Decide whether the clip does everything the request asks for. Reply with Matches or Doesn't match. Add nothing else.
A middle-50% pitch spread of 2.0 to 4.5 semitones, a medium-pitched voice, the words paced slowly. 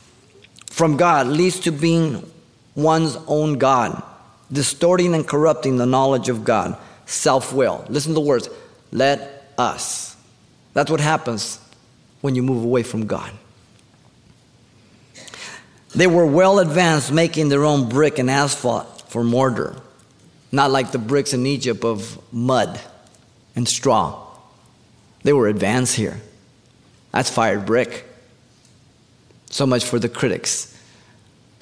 Doesn't match